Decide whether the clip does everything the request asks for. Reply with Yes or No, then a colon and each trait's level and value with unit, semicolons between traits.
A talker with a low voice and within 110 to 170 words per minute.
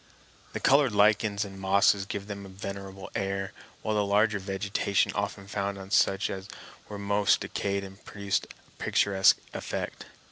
Yes: low, 100 Hz; average, 150 wpm